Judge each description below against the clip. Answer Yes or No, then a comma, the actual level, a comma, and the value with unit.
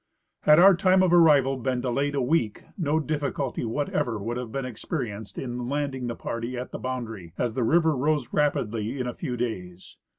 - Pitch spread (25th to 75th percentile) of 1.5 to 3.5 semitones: No, average, 3.9 semitones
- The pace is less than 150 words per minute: No, average, 190 wpm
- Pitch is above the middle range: No, low, 130 Hz